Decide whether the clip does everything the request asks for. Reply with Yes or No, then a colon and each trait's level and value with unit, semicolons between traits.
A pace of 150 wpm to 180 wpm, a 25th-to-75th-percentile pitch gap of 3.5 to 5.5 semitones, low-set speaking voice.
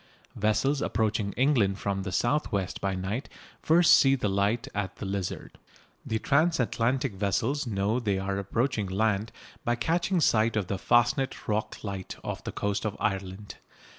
Yes: average, 160 wpm; average, 4.3 semitones; low, 110 Hz